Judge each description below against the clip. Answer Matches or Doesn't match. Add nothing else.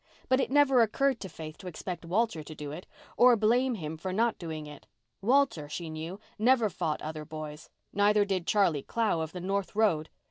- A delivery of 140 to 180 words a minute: Doesn't match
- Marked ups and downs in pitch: Matches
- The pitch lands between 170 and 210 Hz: Matches